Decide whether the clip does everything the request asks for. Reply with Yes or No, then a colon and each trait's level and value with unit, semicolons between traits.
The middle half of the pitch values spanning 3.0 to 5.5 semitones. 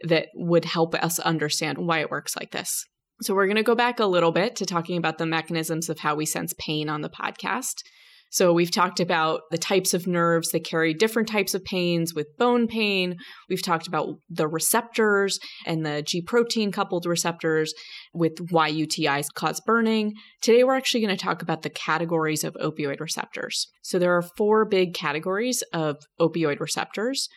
Yes: average, 4.4 semitones